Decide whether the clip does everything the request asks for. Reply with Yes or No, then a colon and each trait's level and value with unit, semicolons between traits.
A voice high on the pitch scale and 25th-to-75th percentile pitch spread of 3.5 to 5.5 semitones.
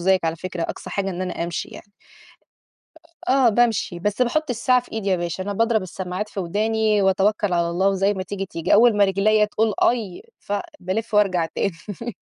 No: high, 200 Hz; average, 2.9 semitones